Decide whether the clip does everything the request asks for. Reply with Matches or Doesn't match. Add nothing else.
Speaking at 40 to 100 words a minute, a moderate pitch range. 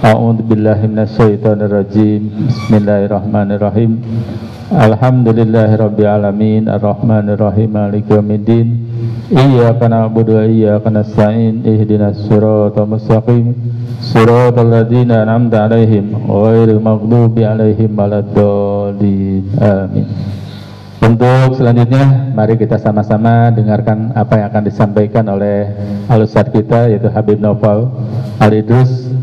Doesn't match